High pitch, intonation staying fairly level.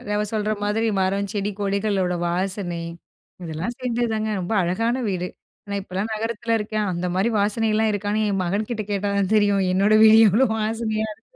Yes: high, 205 Hz; narrow, 2.2 semitones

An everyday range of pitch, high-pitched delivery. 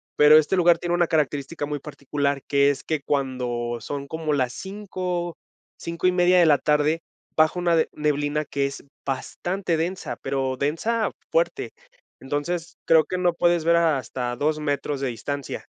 No: average, 3.6 semitones; medium, 150 Hz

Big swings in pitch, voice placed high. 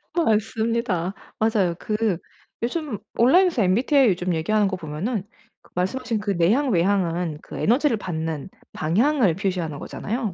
No: average, 4.9 semitones; high, 205 Hz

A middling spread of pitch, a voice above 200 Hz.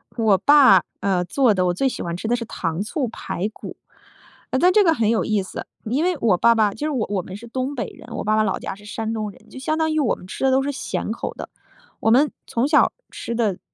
Yes: average, 4.9 semitones; high, 230 Hz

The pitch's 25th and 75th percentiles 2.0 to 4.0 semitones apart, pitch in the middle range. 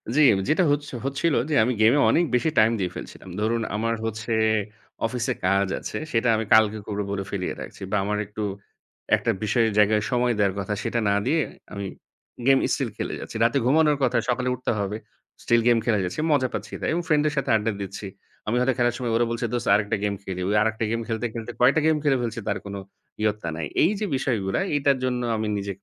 No: average, 3.5 semitones; low, 115 Hz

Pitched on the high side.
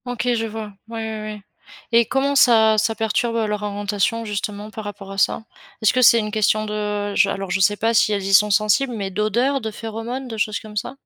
Yes: high, 215 Hz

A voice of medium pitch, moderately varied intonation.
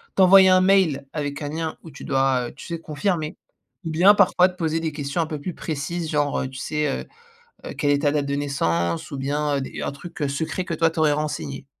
Yes: medium, 150 Hz; average, 3.0 semitones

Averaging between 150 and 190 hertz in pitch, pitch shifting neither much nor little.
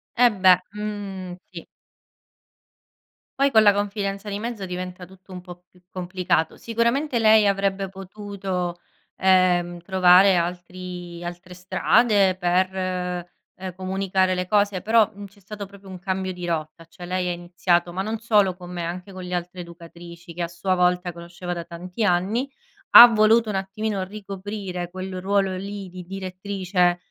No: medium, 185 Hz; narrow, 2.1 semitones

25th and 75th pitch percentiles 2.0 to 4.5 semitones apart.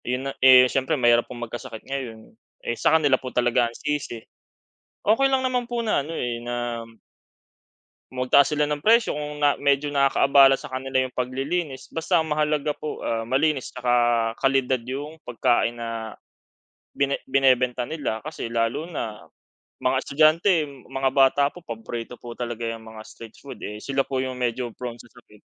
Yes: average, 3.6 semitones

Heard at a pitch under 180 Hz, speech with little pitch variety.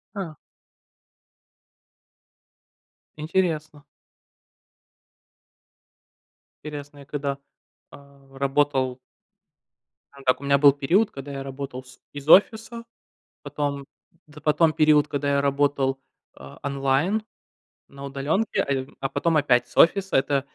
Yes: medium, 140 Hz; narrow, 2.0 semitones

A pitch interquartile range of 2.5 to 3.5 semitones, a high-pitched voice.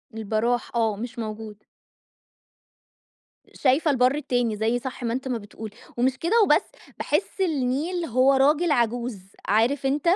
No: average, 4.0 semitones; very high, 250 Hz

